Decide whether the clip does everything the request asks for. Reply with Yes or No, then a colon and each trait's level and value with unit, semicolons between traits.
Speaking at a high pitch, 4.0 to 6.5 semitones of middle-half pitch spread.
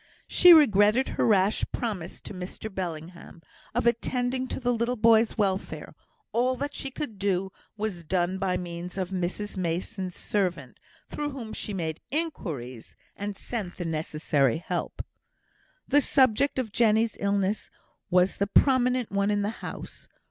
Yes: high, 205 Hz; average, 4.8 semitones